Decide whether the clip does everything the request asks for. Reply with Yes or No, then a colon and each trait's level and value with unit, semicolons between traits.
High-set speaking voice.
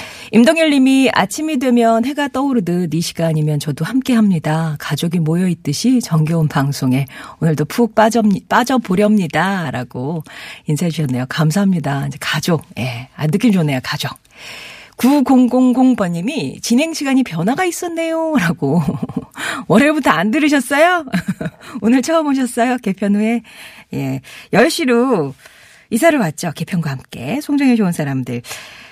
Yes: high, 200 Hz